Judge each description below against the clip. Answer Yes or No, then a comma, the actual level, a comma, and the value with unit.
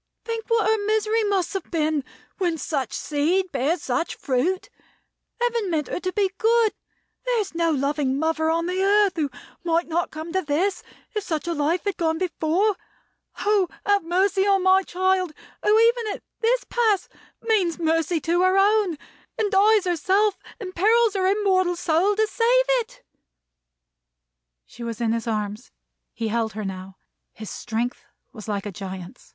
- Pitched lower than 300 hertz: No, very high, 360 Hz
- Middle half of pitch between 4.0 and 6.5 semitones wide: Yes, average, 5.2 semitones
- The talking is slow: No, average, 170 wpm